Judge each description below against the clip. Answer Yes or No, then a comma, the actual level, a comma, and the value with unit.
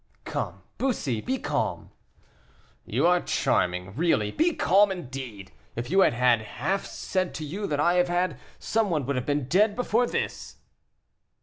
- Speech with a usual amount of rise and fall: No, wide, 7.5 semitones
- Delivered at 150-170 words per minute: Yes, average, 165 wpm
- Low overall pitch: No, medium, 170 Hz